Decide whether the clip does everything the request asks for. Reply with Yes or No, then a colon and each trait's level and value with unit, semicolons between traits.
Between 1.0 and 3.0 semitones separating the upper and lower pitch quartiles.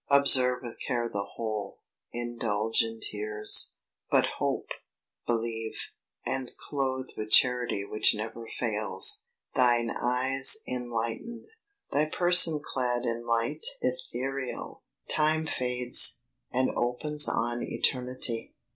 Yes: average, 2.7 semitones